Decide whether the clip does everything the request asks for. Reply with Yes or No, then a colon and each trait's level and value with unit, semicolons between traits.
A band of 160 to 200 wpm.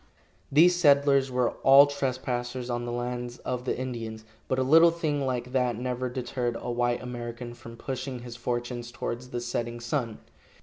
Yes: average, 170 wpm